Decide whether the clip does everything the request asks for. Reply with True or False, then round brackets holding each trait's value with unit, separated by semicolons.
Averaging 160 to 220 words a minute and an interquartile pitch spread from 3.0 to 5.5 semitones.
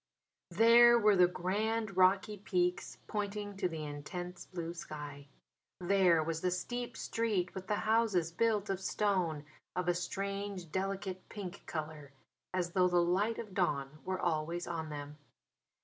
False (150 wpm; 3.3 semitones)